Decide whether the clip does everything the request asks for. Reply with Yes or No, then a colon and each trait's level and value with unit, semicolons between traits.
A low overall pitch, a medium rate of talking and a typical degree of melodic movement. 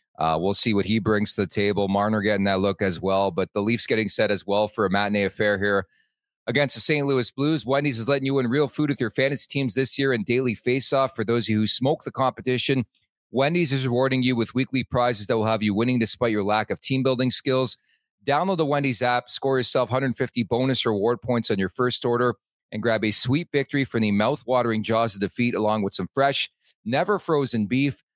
No: low, 120 Hz; fast, 230 wpm; average, 4.0 semitones